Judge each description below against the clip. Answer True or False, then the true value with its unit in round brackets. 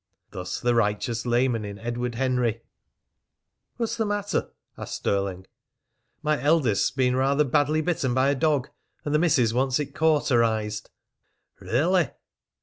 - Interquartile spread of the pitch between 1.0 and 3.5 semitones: False (4.6 semitones)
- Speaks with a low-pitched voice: True (130 Hz)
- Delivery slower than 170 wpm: True (135 wpm)